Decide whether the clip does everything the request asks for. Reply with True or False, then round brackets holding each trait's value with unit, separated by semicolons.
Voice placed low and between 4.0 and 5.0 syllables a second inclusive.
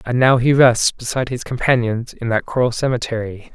False (120 Hz; 5.5 syllables/s)